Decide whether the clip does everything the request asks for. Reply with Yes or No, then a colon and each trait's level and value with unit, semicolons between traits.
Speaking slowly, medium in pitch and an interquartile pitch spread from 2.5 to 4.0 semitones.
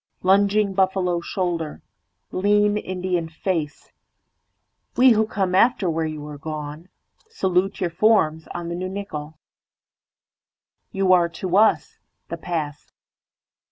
Yes: slow, 90 wpm; medium, 180 Hz; average, 3.4 semitones